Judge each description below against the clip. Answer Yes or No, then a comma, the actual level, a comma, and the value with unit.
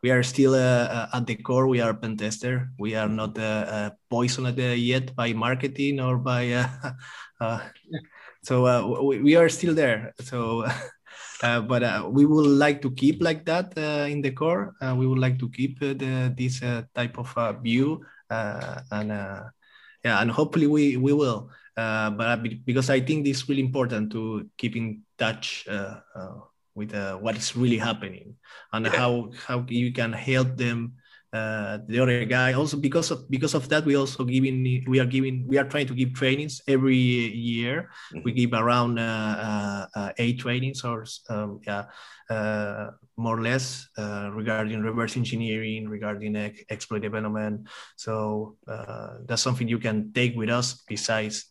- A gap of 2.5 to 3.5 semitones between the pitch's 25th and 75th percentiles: Yes, average, 3.0 semitones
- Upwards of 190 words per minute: No, average, 185 wpm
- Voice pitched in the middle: No, low, 120 Hz